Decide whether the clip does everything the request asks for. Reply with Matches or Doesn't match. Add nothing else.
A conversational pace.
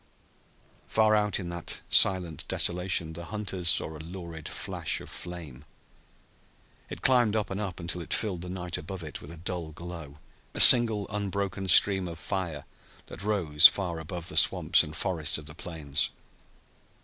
Matches